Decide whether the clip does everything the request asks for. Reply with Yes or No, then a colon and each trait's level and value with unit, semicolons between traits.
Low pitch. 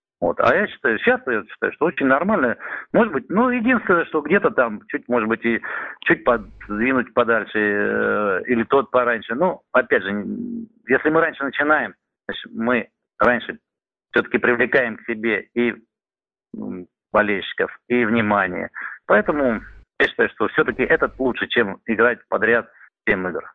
Yes: low, 120 Hz